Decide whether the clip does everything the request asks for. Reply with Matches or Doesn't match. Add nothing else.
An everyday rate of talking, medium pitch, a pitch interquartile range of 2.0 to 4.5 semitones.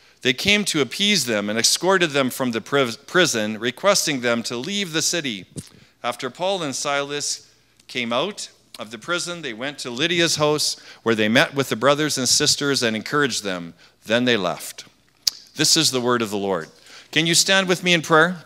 Doesn't match